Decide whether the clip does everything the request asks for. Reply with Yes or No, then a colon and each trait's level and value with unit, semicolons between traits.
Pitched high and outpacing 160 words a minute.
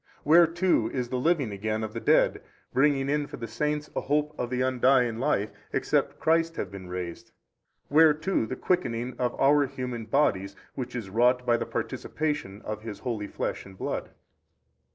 No: low, 125 Hz; average, 180 wpm